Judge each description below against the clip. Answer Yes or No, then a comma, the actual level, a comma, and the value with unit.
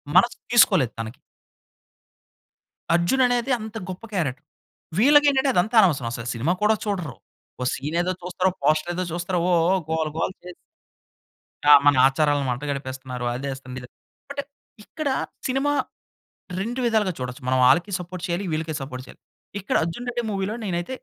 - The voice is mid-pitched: Yes, medium, 175 Hz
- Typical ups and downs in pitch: No, wide, 7.3 semitones